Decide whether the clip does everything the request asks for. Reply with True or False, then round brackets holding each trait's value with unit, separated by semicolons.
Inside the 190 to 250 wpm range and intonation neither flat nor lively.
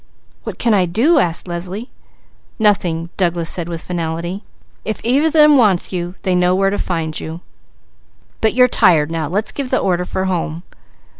False (175 wpm; 4.3 semitones)